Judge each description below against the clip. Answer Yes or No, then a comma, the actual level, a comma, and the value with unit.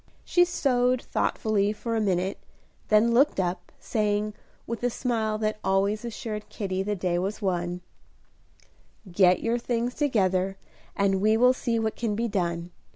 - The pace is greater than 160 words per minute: No, average, 155 wpm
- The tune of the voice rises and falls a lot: No, average, 3.4 semitones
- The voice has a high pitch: Yes, high, 210 Hz